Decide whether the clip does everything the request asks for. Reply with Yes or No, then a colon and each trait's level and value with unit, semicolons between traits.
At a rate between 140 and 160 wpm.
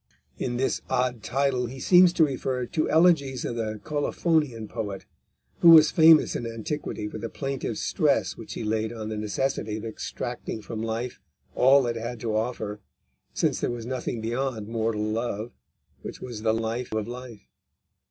No: average, 170 wpm